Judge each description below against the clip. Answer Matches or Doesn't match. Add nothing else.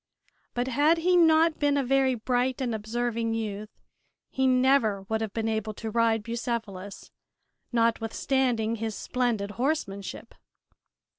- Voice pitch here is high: Matches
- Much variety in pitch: Doesn't match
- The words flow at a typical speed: Doesn't match